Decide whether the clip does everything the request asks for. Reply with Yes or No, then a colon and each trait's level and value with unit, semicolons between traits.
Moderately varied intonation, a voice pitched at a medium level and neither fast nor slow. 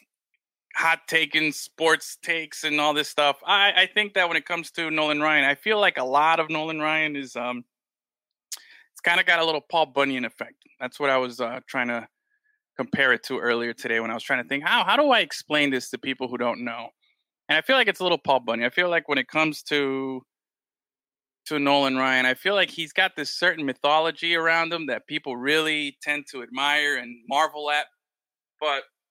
No: average, 3.5 semitones; medium, 150 Hz; fast, 215 wpm